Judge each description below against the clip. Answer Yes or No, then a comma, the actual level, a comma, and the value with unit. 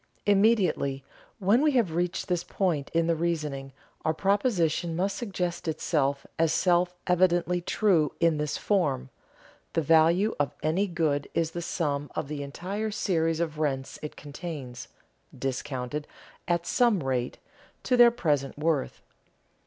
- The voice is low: No, medium, 165 Hz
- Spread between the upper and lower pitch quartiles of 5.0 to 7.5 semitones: No, average, 4.0 semitones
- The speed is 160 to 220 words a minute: No, average, 140 wpm